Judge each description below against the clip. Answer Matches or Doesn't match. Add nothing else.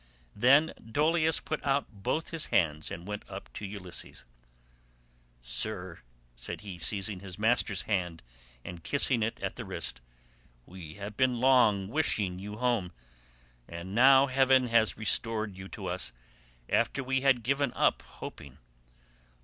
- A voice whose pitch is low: Matches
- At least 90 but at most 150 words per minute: Matches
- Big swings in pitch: Matches